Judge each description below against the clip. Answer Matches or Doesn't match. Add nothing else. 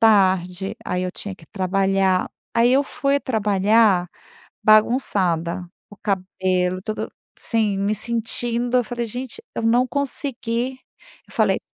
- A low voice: Doesn't match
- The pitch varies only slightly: Doesn't match